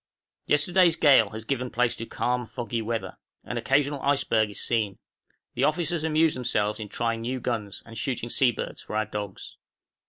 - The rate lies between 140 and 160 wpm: No, average, 175 wpm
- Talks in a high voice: No, low, 120 Hz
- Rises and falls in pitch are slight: No, average, 4.2 semitones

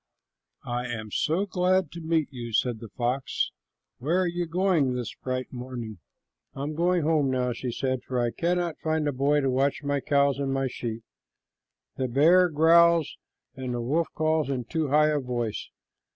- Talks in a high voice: No, medium, 140 Hz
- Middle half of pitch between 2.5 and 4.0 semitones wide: No, average, 4.5 semitones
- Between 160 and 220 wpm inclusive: Yes, average, 180 wpm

